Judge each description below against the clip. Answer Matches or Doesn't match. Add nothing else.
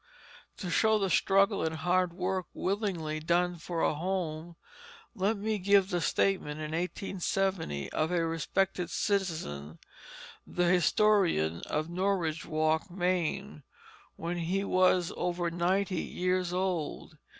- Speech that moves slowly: Matches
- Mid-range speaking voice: Matches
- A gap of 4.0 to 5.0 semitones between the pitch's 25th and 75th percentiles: Doesn't match